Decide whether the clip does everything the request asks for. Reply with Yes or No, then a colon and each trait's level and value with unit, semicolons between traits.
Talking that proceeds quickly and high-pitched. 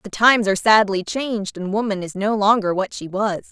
Yes: fast, 220 wpm; high, 205 Hz